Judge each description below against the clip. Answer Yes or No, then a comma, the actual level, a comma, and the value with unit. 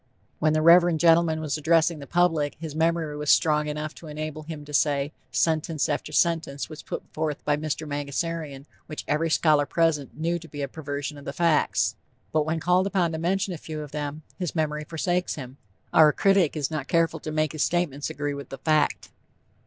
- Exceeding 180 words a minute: Yes, average, 200 wpm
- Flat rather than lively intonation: Yes, narrow, 2.0 semitones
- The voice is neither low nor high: Yes, medium, 155 Hz